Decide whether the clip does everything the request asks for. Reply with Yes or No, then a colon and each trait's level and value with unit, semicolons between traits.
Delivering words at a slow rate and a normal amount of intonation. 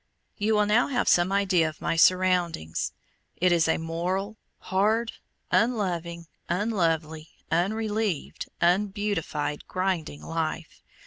Yes: slow, 110 wpm; average, 4.0 semitones